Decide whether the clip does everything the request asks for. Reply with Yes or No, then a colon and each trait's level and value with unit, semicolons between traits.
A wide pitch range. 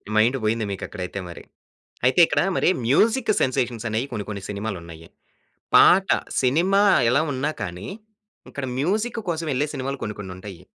Yes: wide, 6.4 semitones